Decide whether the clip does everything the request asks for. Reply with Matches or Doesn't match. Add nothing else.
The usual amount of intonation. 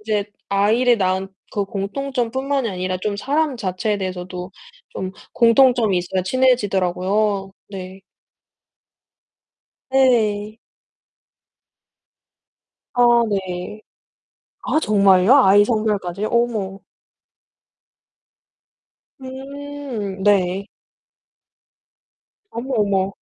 Matches